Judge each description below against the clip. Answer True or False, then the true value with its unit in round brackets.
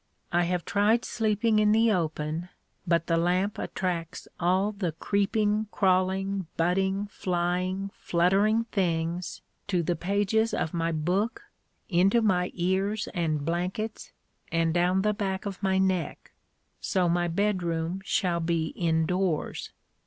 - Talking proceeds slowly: True (130 wpm)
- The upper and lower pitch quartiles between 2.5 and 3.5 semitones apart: True (2.9 semitones)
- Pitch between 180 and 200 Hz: True (185 Hz)